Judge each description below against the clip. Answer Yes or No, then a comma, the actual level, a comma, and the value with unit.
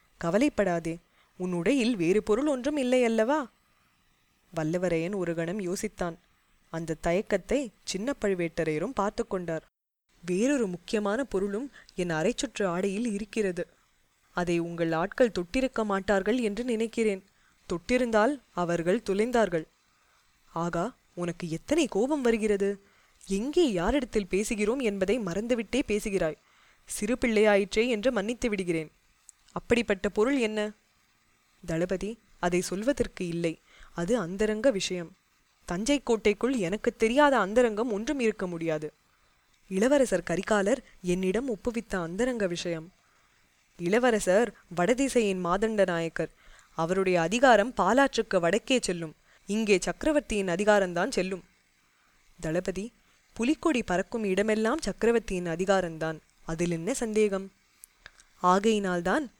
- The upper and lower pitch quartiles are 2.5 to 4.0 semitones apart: No, average, 4.8 semitones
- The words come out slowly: No, average, 100 wpm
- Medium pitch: No, high, 200 Hz